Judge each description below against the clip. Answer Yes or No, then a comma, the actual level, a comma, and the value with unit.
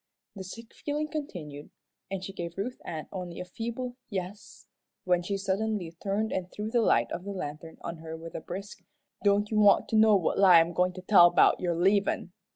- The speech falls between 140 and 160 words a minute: No, fast, 205 wpm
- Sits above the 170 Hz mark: Yes, high, 190 Hz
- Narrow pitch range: No, average, 3.4 semitones